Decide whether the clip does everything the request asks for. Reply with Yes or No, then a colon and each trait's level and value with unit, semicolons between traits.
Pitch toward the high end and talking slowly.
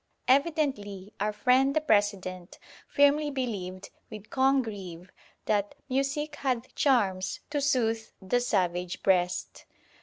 Yes: high, 225 Hz; slow, 110 wpm